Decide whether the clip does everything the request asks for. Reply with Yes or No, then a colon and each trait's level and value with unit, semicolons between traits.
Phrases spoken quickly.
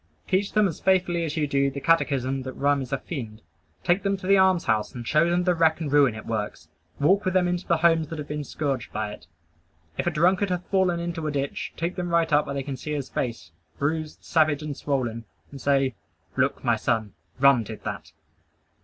Yes: fast, 225 wpm